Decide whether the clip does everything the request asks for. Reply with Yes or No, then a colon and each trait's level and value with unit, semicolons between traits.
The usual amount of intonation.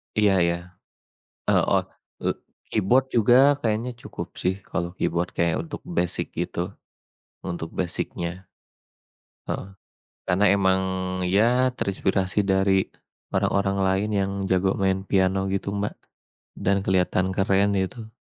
No: narrow, 2.1 semitones